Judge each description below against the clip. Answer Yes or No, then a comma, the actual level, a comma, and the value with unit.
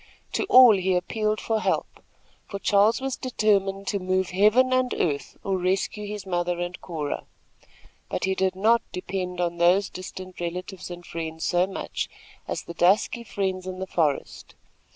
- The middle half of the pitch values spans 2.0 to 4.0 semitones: Yes, average, 2.8 semitones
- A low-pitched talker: No, high, 190 Hz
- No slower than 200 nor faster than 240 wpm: No, average, 165 wpm